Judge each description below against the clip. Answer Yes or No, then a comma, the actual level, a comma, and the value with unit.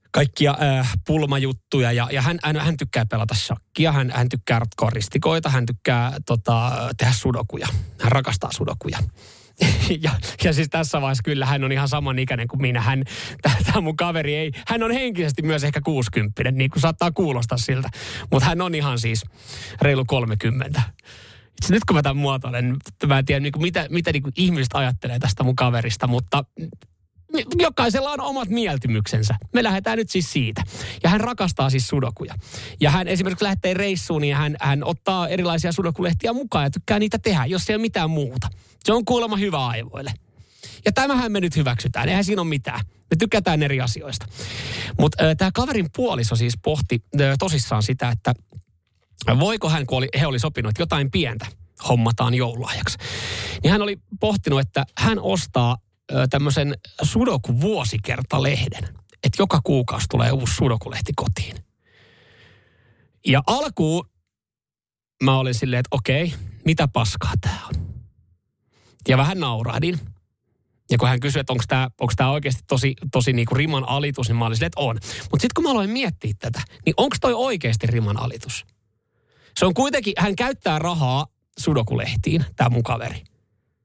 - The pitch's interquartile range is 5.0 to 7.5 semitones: Yes, average, 5.3 semitones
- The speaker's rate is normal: No, fast, 160 wpm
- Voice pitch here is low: Yes, low, 130 Hz